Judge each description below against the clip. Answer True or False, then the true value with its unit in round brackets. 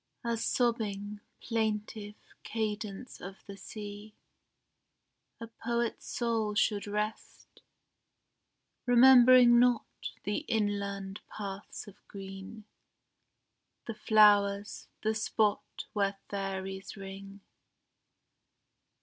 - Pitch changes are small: True (2.1 semitones)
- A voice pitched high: True (210 Hz)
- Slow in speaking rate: True (80 wpm)